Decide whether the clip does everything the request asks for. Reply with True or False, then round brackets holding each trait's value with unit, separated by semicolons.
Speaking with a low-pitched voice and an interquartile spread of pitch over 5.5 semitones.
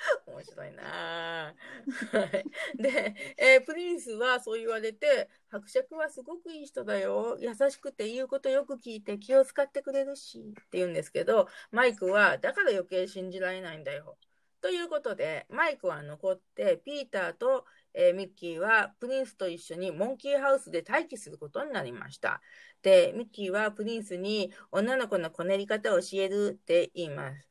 False (245 Hz; 6.7 semitones)